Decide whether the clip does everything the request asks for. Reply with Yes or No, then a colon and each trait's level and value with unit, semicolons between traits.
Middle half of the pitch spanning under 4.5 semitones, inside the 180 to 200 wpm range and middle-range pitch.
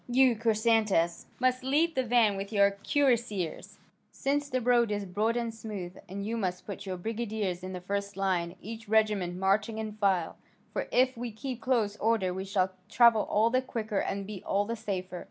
No: average, 3.3 semitones; average, 190 wpm; high, 215 Hz